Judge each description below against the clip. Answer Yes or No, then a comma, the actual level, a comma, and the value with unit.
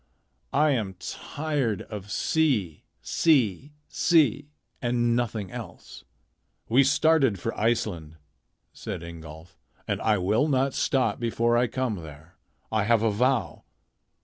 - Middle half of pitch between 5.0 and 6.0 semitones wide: Yes, average, 5.3 semitones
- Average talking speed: No, slow, 120 wpm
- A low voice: Yes, low, 115 Hz